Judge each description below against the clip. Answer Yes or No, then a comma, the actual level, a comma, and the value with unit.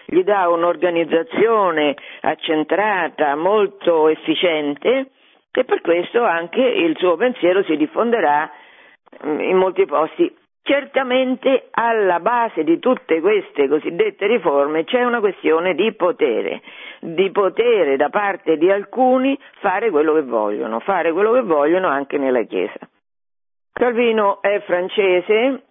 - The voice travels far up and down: Yes, wide, 7.8 semitones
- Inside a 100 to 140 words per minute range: Yes, average, 120 wpm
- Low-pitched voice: No, high, 210 Hz